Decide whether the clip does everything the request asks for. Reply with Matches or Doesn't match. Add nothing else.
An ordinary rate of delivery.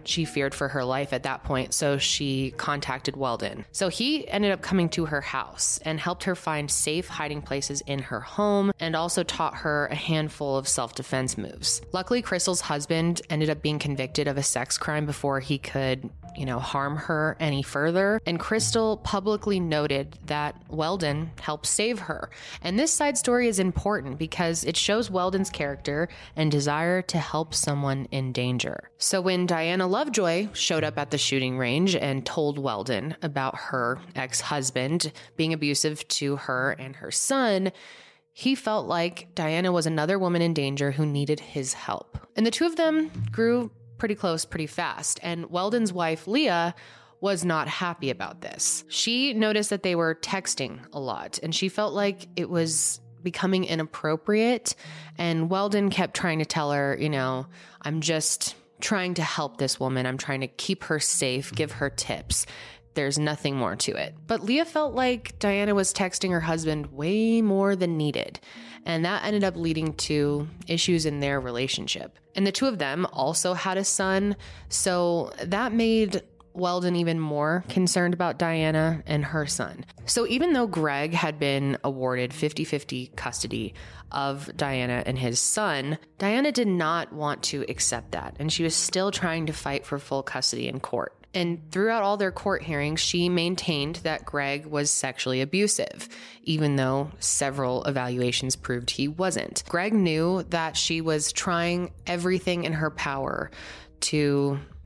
Matches